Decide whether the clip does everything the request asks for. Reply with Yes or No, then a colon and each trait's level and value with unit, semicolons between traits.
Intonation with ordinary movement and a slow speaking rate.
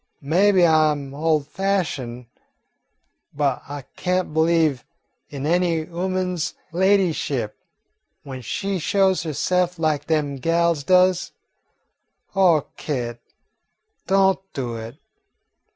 Yes: average, 4.3 semitones; slow, 100 wpm